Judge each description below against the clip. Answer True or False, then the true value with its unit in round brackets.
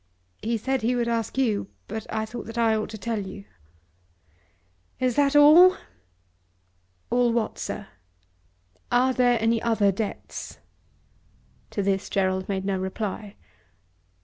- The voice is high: True (225 Hz)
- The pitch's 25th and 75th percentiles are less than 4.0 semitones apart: True (3.4 semitones)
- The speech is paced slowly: True (130 wpm)